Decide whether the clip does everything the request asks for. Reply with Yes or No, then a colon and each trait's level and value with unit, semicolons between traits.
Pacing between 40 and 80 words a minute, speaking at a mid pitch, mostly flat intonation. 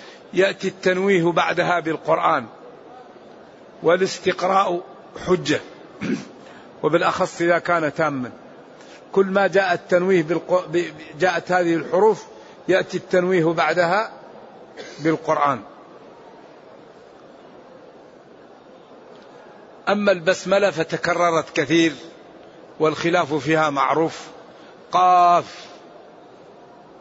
Yes: slow, 65 wpm; medium, 175 Hz; narrow, 2.3 semitones